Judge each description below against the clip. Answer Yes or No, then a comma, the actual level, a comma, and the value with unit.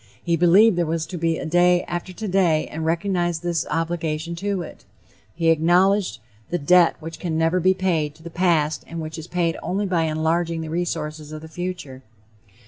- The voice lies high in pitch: No, medium, 170 Hz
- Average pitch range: No, narrow, 1.9 semitones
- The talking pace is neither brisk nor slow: Yes, average, 190 wpm